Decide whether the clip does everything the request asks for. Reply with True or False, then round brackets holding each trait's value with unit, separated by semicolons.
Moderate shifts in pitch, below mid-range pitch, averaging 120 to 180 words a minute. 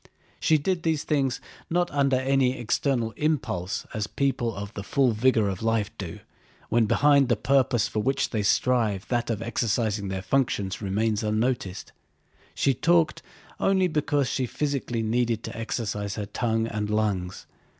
True (4.4 semitones; 120 Hz; 155 wpm)